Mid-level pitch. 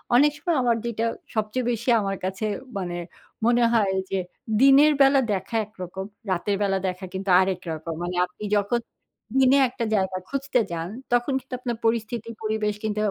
No: high, 215 Hz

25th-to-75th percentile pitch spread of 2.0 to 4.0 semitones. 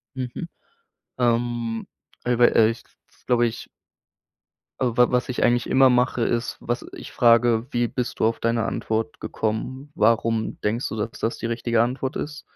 No: narrow, 1.3 semitones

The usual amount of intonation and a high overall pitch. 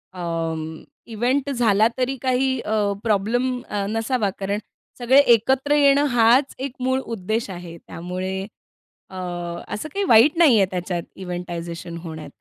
No: wide, 6.4 semitones; high, 220 Hz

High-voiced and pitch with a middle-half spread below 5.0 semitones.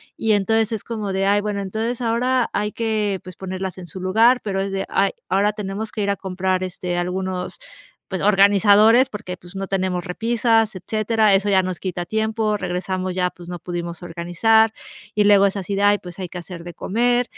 Yes: high, 195 Hz; average, 2.9 semitones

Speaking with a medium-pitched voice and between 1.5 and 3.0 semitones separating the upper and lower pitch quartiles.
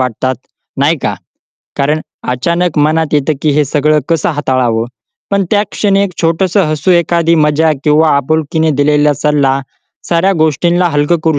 Yes: medium, 155 Hz; average, 2.7 semitones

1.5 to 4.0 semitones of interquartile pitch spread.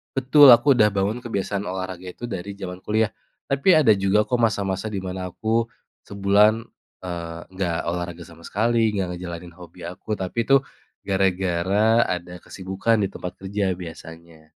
Yes: average, 3.4 semitones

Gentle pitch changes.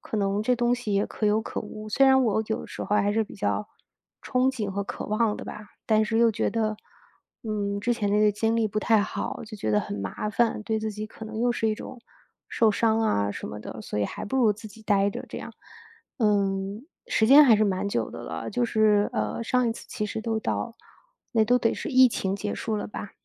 Yes: narrow, 2.1 semitones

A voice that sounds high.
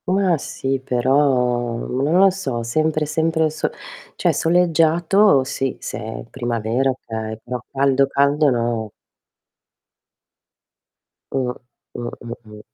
No: low, 135 Hz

